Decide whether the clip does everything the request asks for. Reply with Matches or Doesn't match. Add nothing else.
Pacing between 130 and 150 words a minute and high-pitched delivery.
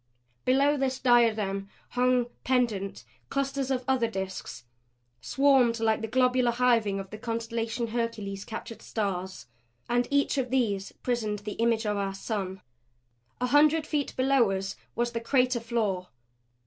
Matches